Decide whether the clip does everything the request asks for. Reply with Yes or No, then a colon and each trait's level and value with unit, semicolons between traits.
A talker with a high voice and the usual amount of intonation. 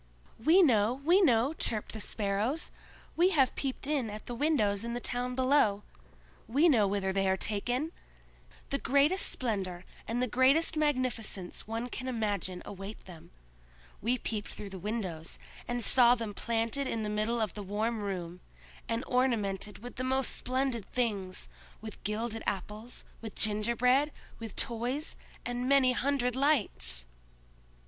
Yes: high, 230 Hz; average, 3.9 semitones